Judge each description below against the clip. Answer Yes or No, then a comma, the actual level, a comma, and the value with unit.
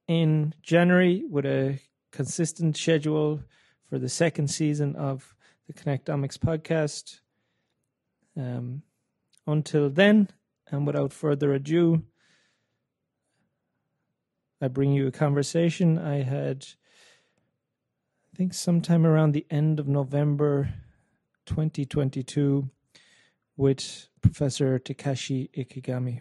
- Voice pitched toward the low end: No, medium, 145 Hz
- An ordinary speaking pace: No, slow, 95 wpm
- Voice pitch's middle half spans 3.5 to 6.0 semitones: No, average, 2.9 semitones